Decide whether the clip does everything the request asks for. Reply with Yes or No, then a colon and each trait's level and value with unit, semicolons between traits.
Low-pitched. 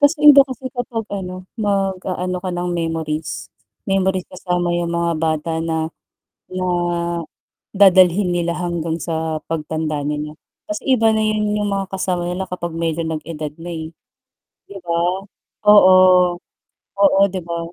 No: medium, 175 Hz